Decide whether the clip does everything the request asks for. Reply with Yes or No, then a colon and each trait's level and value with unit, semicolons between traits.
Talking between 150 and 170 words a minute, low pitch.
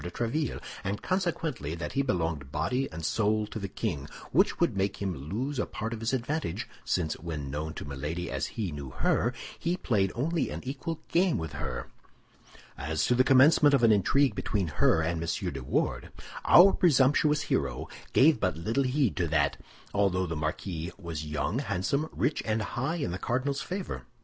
No: average, 185 wpm; low, 100 Hz